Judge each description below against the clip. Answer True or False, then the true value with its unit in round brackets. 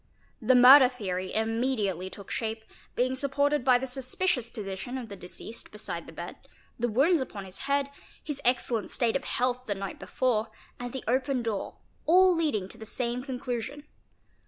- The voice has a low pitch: False (245 Hz)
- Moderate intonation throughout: True (3.6 semitones)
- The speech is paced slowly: False (170 wpm)